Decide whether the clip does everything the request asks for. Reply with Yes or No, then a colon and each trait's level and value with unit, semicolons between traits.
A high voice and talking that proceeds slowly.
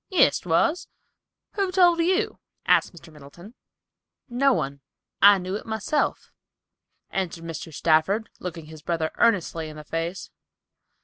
No: medium, 180 Hz; slow, 130 wpm